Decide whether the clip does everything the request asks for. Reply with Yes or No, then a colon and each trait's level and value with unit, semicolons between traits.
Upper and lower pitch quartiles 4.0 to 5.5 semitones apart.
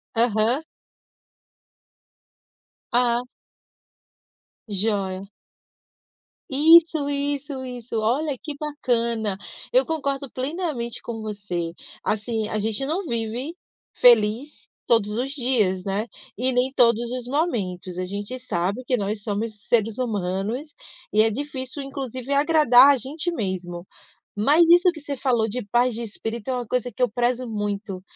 Yes: average, 4.6 semitones